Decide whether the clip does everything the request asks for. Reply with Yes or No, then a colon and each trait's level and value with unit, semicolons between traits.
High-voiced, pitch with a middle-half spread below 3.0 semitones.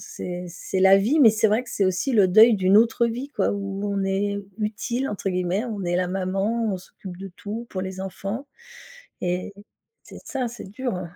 No: high, 200 Hz; average, 3.3 semitones